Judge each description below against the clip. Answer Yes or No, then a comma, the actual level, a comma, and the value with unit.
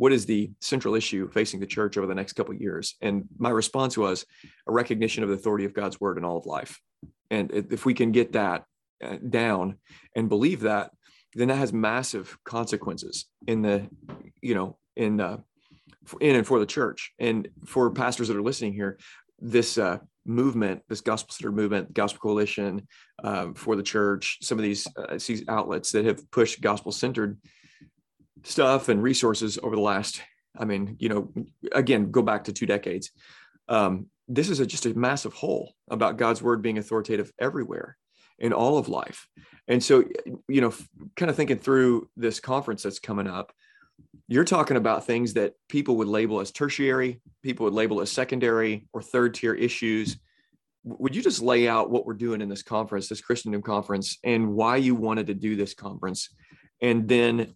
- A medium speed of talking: Yes, average, 185 wpm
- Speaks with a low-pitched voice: Yes, low, 110 Hz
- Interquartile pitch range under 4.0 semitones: Yes, average, 2.8 semitones